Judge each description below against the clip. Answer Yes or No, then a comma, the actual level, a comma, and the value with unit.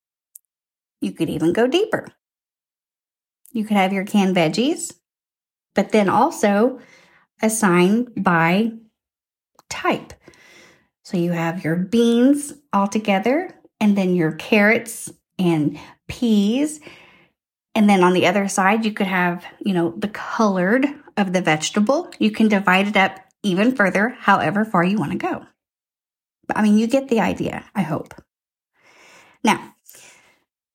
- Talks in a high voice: Yes, high, 205 Hz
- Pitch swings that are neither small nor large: Yes, average, 4.2 semitones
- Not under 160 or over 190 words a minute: No, slow, 135 wpm